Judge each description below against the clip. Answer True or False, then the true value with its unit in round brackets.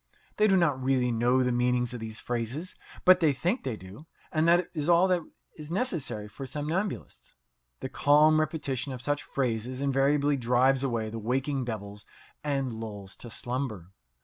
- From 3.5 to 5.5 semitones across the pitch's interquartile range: True (4.4 semitones)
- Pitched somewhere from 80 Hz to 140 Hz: True (135 Hz)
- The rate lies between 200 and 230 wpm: False (170 wpm)